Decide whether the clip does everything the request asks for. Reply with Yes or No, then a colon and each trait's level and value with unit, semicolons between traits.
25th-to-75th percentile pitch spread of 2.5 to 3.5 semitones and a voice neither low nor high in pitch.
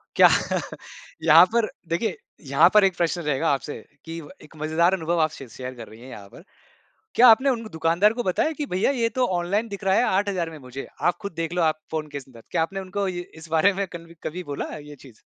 No: average, 4.4 semitones; medium, 170 Hz